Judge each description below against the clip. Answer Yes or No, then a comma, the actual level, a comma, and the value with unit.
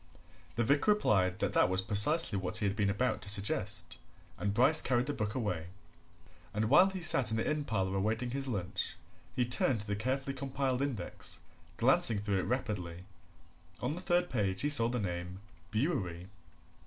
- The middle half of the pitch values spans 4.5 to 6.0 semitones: Yes, wide, 5.4 semitones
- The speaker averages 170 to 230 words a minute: Yes, average, 180 wpm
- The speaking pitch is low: Yes, low, 110 Hz